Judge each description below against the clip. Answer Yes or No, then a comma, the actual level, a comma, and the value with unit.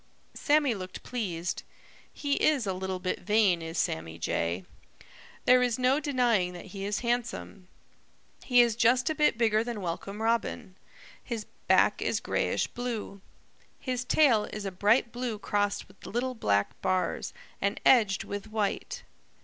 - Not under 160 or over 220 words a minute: No, average, 150 wpm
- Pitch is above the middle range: Yes, high, 215 Hz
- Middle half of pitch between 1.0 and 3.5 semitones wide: No, average, 4.5 semitones